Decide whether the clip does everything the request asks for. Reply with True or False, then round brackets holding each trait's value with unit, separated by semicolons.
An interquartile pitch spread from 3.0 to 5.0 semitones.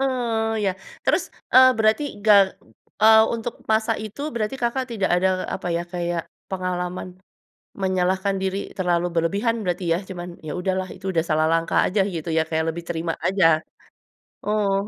True (3.8 semitones)